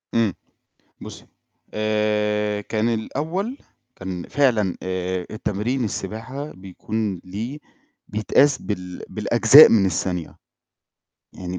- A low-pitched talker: Yes, low, 105 Hz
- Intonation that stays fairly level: No, average, 3.8 semitones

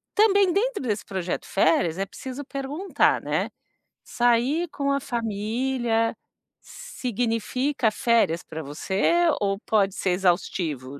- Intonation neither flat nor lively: No, wide, 6.1 semitones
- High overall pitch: Yes, high, 230 Hz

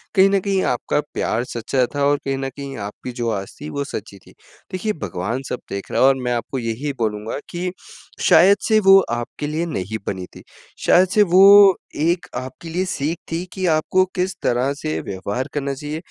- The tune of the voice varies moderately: No, wide, 7.2 semitones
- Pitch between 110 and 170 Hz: Yes, medium, 140 Hz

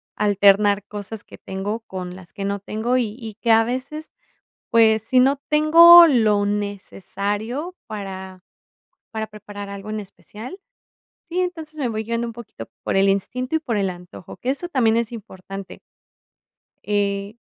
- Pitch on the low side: No, high, 215 Hz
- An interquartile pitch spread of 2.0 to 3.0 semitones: No, average, 3.9 semitones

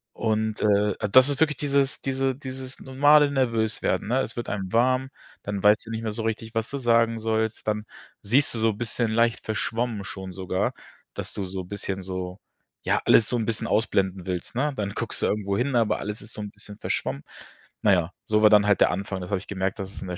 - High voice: No, low, 110 Hz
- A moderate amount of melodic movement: Yes, average, 3.2 semitones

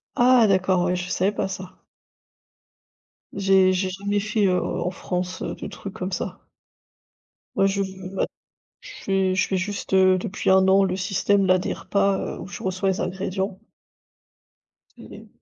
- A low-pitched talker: No, high, 190 Hz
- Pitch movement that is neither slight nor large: No, narrow, 1.1 semitones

